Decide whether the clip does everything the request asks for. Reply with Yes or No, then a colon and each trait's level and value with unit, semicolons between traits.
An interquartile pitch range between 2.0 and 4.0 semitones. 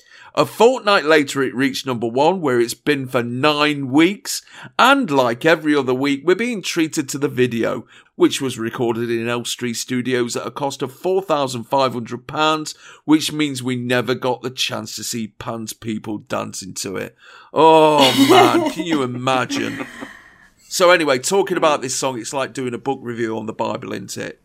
No: average, 4.5 semitones